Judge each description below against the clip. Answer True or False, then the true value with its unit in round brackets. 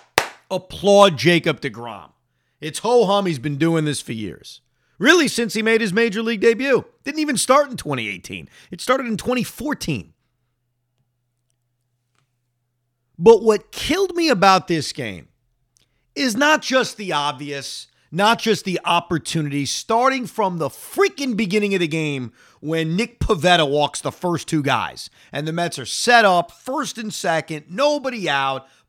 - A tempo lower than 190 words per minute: True (150 wpm)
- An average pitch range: False (8.9 semitones)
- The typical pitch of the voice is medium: True (170 Hz)